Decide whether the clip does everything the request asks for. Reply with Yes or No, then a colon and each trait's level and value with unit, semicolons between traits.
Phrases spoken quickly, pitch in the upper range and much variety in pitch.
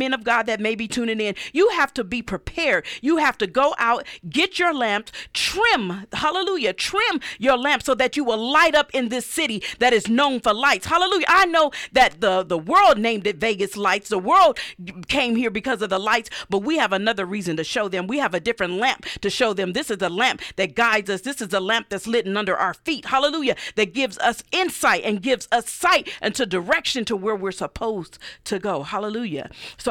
Yes: fast, 225 wpm; high, 235 Hz; wide, 5.7 semitones